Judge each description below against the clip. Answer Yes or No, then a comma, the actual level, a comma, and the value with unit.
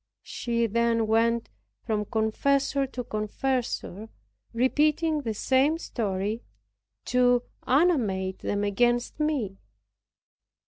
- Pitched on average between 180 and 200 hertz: No, high, 235 Hz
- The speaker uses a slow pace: Yes, slow, 90 wpm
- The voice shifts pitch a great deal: No, average, 3.8 semitones